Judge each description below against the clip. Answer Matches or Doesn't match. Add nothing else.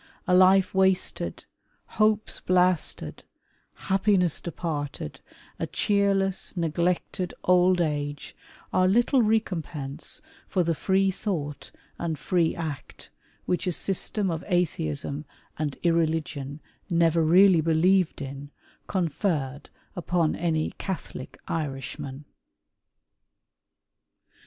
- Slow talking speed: Matches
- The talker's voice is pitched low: Doesn't match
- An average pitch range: Matches